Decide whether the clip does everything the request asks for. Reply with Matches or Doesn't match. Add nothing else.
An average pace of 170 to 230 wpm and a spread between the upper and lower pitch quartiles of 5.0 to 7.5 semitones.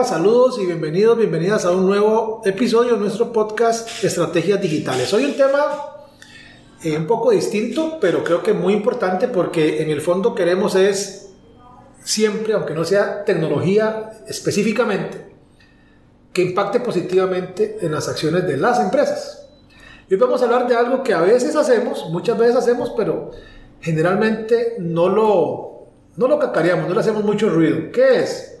Doesn't match